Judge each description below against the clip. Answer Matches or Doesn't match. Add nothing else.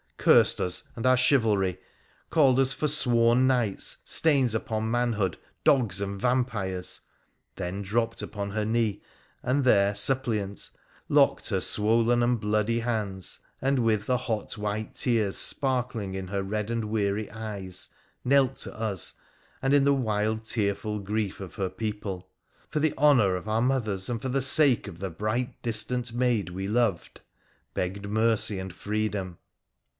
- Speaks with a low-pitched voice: Matches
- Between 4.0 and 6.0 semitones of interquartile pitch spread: Doesn't match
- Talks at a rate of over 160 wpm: Doesn't match